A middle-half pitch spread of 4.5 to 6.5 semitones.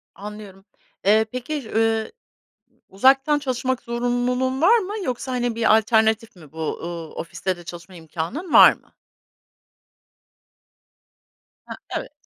Yes: average, 5.1 semitones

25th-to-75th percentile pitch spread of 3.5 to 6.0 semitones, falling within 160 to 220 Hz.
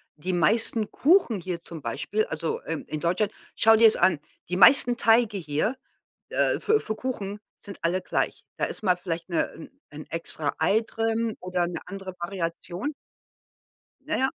Yes: average, 4.8 semitones; high, 190 Hz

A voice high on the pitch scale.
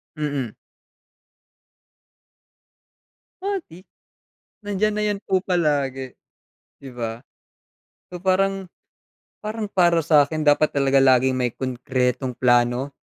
No: medium, 145 Hz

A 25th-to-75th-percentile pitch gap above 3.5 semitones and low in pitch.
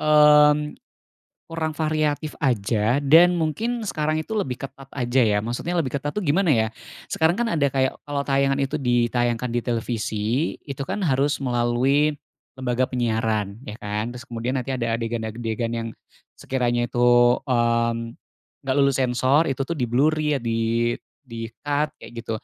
Yes: average, 4.0 semitones; low, 130 Hz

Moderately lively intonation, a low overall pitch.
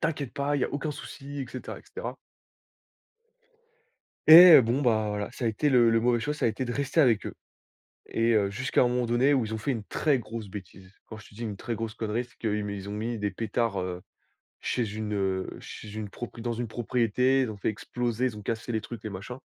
Yes: average, 3.2 semitones; low, 115 Hz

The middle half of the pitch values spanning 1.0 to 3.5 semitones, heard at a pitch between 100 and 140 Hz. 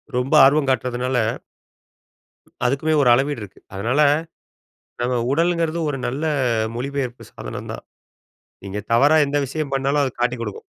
Yes: average, 3.0 semitones; low, 135 Hz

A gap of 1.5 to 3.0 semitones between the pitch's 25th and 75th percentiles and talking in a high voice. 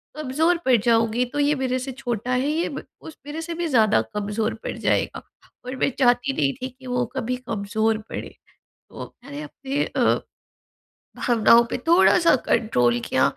No: average, 4.1 semitones; very high, 250 Hz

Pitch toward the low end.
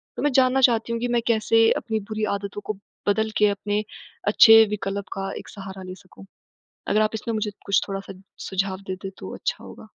No: high, 210 Hz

